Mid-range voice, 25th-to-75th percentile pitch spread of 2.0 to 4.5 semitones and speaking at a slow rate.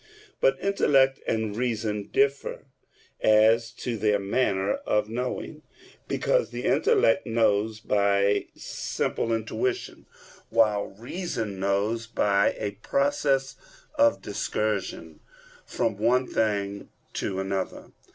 No: low, 110 Hz; average, 4.0 semitones; slow, 105 wpm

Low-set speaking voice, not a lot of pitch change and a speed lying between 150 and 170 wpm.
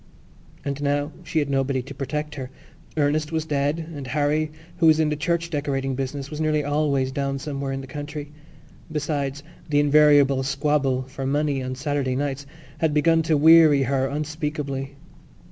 No: medium, 145 Hz; narrow, 1.9 semitones; average, 165 wpm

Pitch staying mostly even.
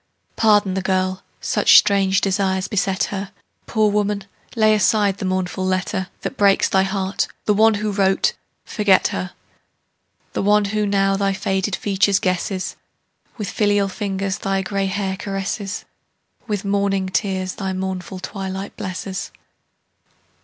Yes: narrow, 1.3 semitones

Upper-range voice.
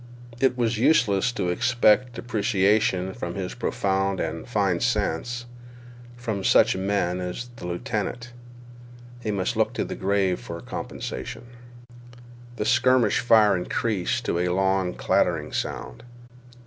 No: low, 100 Hz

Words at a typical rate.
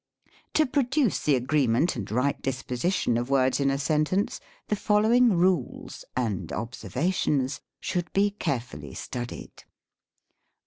No: slow, 130 wpm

